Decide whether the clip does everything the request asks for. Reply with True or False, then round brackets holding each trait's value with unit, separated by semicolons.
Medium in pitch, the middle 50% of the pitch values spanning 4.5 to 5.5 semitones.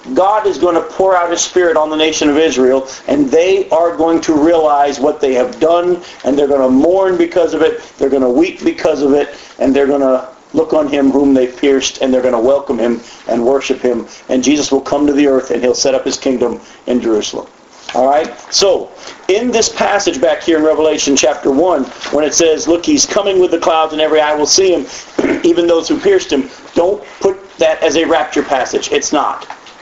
True (155 Hz; 4.9 semitones)